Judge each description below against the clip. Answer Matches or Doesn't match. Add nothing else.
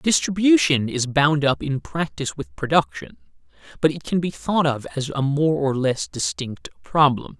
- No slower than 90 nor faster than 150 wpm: Doesn't match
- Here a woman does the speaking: Doesn't match